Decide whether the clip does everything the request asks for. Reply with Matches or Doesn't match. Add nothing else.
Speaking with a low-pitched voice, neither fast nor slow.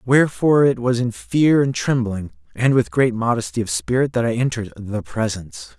Matches